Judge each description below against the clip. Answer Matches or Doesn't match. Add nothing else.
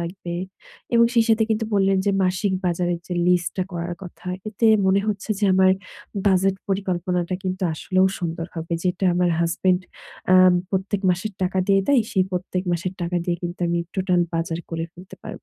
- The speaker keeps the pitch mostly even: Matches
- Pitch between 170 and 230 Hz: Matches